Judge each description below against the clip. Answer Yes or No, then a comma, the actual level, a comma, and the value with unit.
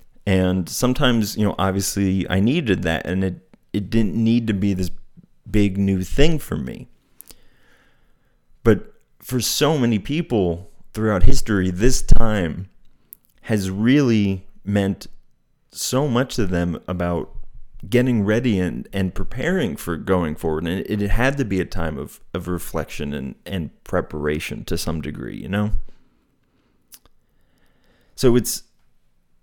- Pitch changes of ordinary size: Yes, average, 4.7 semitones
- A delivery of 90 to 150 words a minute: Yes, slow, 135 wpm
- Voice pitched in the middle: No, low, 100 Hz